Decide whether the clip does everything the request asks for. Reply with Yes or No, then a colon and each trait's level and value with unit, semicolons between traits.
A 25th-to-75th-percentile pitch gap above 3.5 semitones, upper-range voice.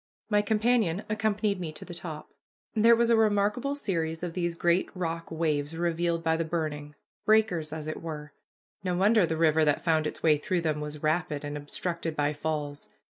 No: average, 4.5 semitones; medium, 165 Hz